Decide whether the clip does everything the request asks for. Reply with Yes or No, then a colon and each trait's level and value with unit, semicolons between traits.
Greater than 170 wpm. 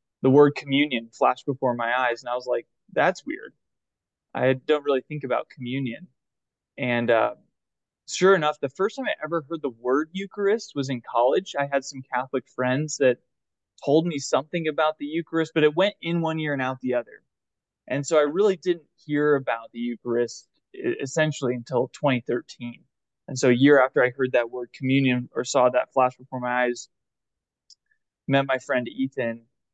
Yes: average, 180 wpm